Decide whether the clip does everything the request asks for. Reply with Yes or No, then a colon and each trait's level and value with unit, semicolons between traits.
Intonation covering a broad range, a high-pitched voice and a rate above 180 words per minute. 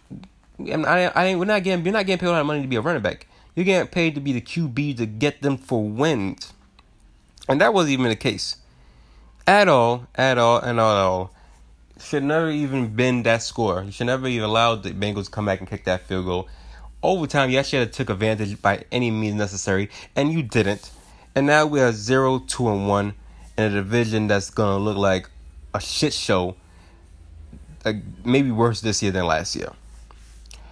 No: wide, 6.3 semitones; low, 110 Hz; fast, 205 wpm